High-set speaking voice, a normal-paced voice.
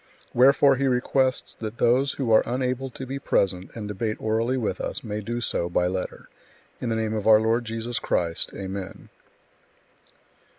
No: low, 115 Hz; average, 165 wpm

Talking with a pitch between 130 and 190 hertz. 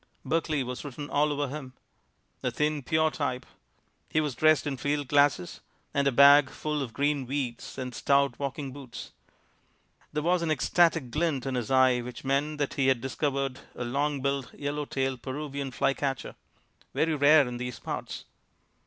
Yes: medium, 140 Hz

